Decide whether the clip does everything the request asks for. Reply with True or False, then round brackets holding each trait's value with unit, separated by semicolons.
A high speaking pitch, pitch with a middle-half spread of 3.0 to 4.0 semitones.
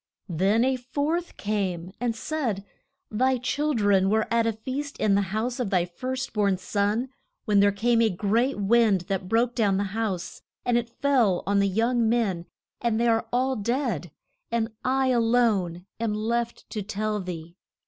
True (220 Hz; 3.5 semitones)